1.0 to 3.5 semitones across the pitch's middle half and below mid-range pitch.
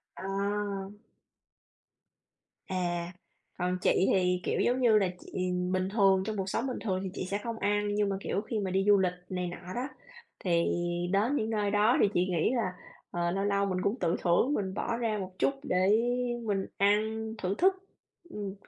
No: average, 2.7 semitones; high, 195 Hz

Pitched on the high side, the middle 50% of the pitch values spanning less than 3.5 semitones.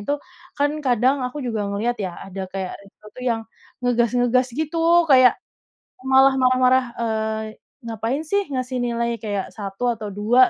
Yes: high, 245 Hz; average, 3.1 semitones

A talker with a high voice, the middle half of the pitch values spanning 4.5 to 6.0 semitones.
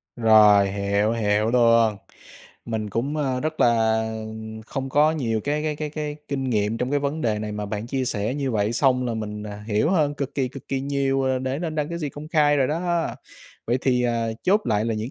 No: low, 125 Hz; average, 4.8 semitones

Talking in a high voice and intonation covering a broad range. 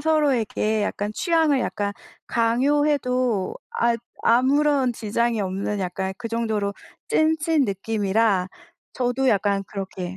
No: high, 230 Hz; average, 4.9 semitones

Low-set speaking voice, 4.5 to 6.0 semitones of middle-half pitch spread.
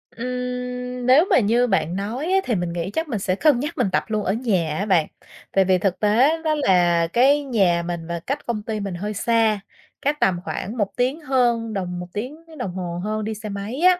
No: high, 215 Hz; average, 5.0 semitones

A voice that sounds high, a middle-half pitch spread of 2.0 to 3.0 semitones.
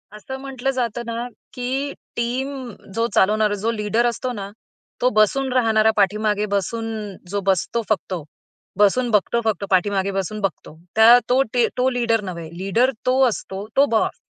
No: high, 225 Hz; average, 3.4 semitones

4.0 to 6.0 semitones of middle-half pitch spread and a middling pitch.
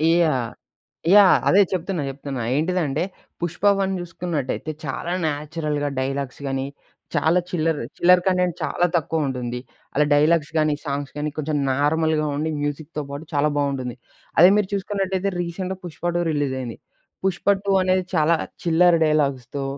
No: average, 3.6 semitones; medium, 155 Hz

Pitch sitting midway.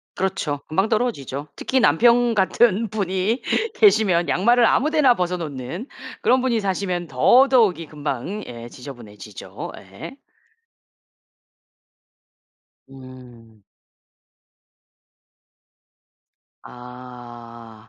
Yes: medium, 175 Hz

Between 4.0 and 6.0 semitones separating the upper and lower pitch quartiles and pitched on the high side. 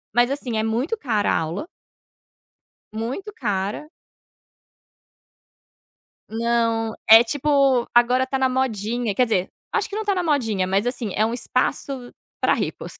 No: average, 3.4 semitones; high, 240 Hz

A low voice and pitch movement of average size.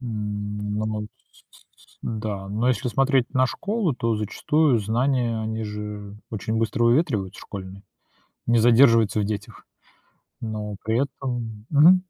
Yes: low, 110 Hz; average, 3.2 semitones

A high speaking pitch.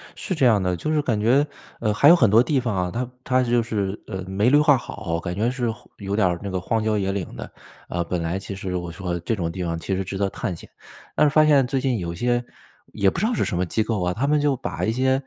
No: low, 105 Hz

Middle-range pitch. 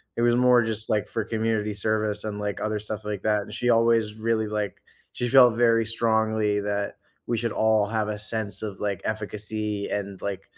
No: low, 110 Hz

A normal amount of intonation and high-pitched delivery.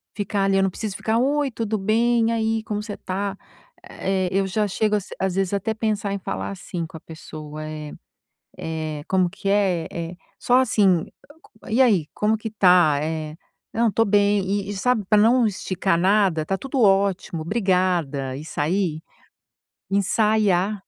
Yes: average, 3.6 semitones; high, 195 Hz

